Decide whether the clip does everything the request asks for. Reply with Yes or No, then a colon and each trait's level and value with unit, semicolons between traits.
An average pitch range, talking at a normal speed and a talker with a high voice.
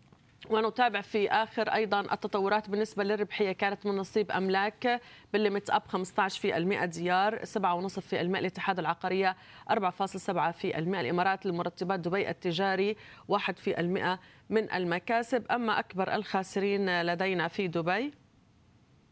No: narrow, 2.3 semitones; average, 125 wpm; high, 195 Hz